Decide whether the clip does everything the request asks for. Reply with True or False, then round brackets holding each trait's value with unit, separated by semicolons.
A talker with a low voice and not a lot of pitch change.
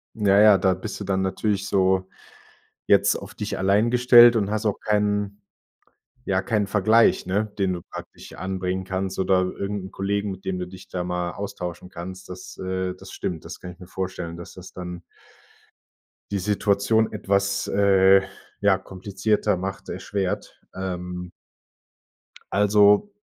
True (95 Hz; 1.8 semitones)